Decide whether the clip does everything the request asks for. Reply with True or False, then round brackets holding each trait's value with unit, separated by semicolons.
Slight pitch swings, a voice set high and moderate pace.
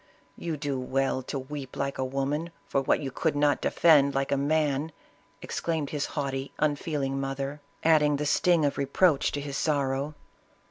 False (1.7 semitones; 140 Hz; 180 wpm)